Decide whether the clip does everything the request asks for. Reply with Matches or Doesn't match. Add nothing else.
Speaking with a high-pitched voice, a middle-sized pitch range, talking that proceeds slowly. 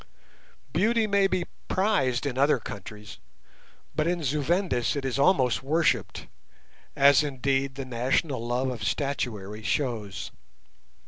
Doesn't match